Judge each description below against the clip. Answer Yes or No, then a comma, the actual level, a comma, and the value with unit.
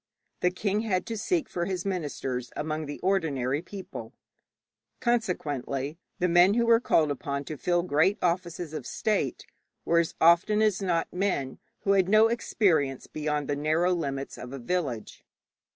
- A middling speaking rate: Yes, average, 160 wpm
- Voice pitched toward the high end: No, medium, 175 Hz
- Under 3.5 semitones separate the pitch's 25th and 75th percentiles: No, average, 5.1 semitones